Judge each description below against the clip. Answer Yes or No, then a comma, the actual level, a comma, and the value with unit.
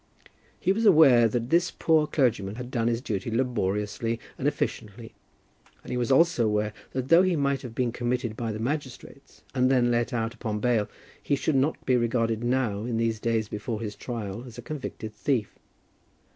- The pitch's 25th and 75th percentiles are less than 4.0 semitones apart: Yes, average, 3.0 semitones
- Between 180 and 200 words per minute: Yes, average, 185 wpm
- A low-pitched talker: Yes, low, 120 Hz